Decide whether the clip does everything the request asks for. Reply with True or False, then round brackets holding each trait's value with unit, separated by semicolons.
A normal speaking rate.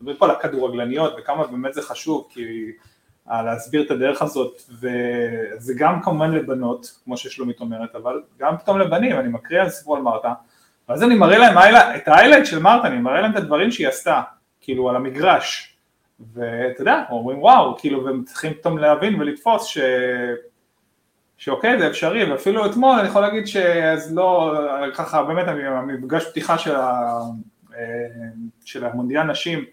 False (155 wpm)